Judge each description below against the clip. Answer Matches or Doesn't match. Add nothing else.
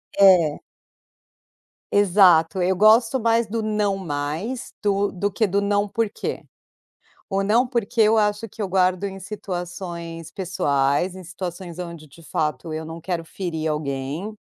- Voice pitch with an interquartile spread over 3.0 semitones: Matches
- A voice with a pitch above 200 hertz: Doesn't match